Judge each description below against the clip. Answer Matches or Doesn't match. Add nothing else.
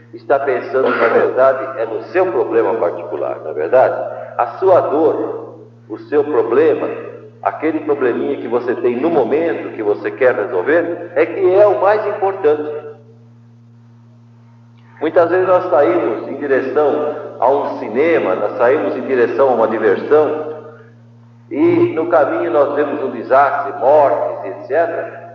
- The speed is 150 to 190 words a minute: Doesn't match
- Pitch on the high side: Doesn't match